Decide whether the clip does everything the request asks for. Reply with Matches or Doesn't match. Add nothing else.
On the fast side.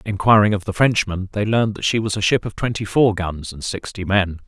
Matches